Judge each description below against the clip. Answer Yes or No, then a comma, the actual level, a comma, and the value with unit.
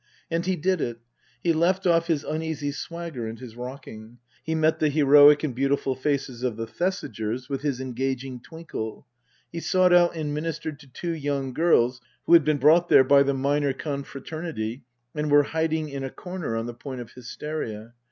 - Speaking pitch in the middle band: Yes, medium, 145 Hz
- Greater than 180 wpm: Yes, average, 190 wpm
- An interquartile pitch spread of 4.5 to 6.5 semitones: No, average, 4.0 semitones